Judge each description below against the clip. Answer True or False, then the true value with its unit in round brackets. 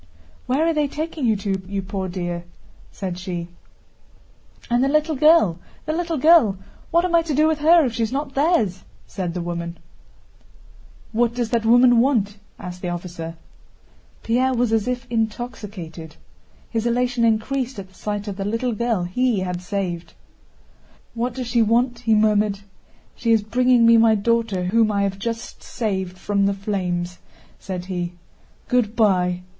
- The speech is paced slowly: False (165 wpm)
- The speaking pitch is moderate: False (220 Hz)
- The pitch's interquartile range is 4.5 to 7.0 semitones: True (4.8 semitones)